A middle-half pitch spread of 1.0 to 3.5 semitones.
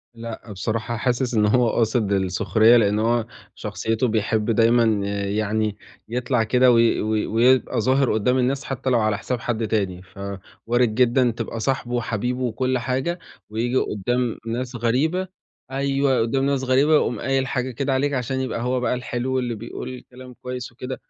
Yes: narrow, 2.6 semitones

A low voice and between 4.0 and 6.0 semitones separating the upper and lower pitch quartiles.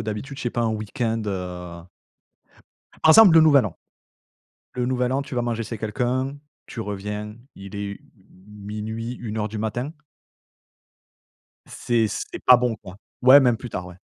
No: low, 110 Hz; average, 3.1 semitones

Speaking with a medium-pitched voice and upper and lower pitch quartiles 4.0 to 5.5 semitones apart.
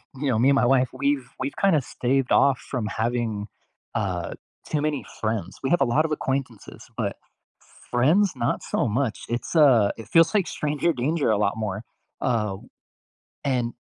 No: low, 125 Hz; average, 4.3 semitones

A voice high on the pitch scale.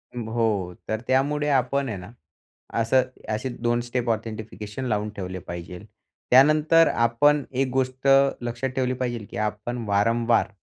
No: low, 120 Hz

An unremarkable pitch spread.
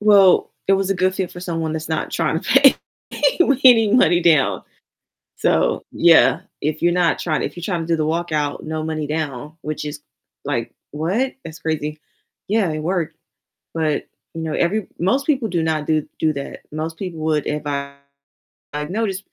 Yes: average, 3.5 semitones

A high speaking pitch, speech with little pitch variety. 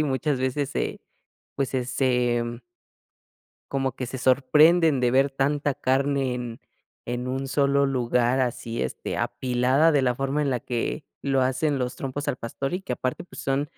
No: low, 130 Hz; narrow, 2.0 semitones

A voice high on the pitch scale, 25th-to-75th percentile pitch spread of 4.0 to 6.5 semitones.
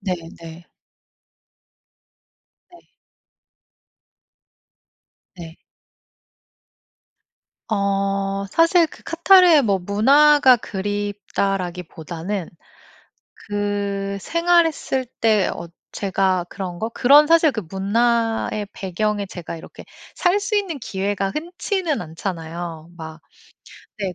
No: high, 200 Hz; wide, 7.3 semitones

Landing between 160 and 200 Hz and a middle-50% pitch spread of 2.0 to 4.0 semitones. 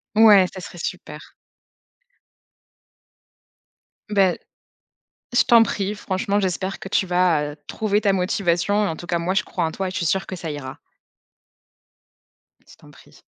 Yes: medium, 185 Hz; average, 2.9 semitones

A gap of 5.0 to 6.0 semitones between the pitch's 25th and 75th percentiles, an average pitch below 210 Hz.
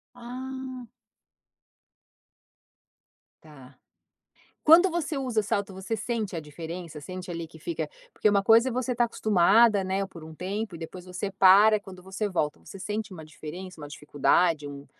Yes: average, 5.3 semitones; high, 190 Hz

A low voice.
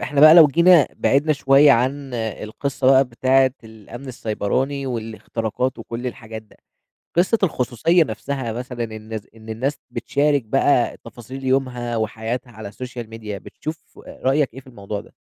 Yes: low, 125 Hz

